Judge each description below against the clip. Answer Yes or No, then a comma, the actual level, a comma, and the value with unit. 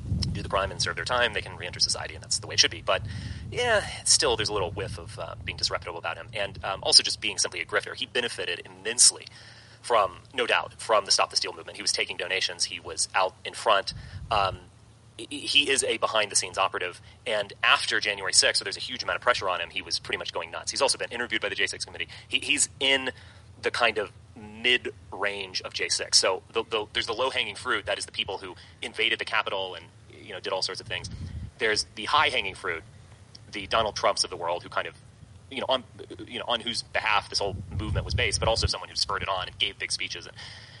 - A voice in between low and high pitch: No, low, 115 Hz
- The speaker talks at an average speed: No, fast, 245 wpm